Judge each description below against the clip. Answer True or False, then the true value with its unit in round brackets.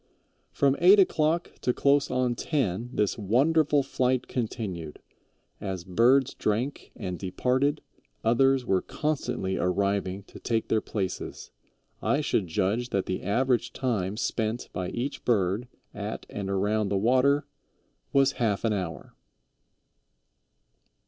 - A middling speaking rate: False (125 wpm)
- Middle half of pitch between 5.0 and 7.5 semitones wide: True (5.4 semitones)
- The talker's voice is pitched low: True (115 Hz)